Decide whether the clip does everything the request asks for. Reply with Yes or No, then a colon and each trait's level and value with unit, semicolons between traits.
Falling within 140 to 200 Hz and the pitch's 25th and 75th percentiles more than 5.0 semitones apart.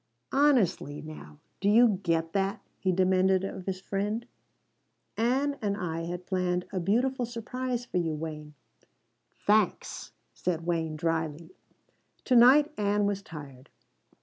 Yes: high, 190 Hz; wide, 5.4 semitones